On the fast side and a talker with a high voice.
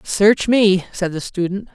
No: average, 170 wpm; high, 195 Hz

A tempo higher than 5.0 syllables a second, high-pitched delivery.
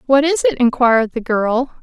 Yes: 5.2 syllables/s; very high, 260 Hz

